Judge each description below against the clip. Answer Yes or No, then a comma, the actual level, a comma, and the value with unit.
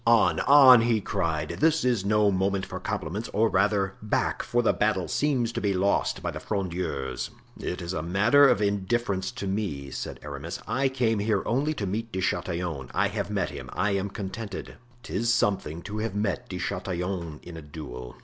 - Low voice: Yes, low, 100 Hz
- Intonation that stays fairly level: No, average, 4.1 semitones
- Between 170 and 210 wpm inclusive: Yes, average, 190 wpm